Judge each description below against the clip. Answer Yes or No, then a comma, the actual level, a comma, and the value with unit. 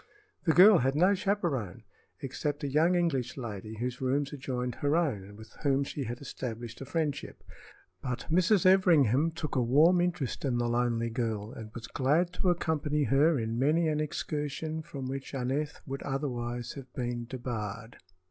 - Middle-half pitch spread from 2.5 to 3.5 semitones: No, average, 4.7 semitones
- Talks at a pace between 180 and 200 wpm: No, average, 170 wpm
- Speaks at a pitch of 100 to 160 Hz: Yes, low, 135 Hz